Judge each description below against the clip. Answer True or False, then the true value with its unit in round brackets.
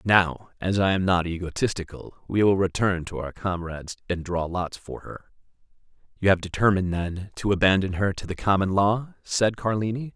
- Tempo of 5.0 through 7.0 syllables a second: True (5.2 syllables/s)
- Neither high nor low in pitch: False (95 Hz)